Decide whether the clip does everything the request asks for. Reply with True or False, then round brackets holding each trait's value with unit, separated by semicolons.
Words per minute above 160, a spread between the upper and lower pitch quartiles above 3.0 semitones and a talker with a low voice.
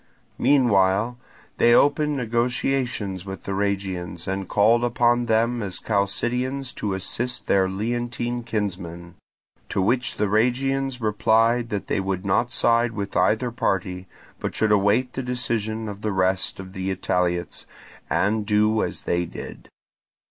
False (140 wpm; 4.0 semitones; 110 Hz)